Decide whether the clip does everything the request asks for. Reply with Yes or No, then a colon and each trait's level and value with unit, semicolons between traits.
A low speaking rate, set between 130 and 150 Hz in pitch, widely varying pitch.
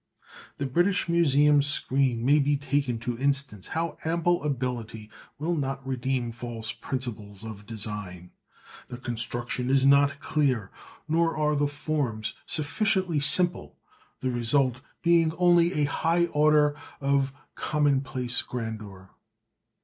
No: slow, 120 wpm; medium, 140 Hz; average, 4.0 semitones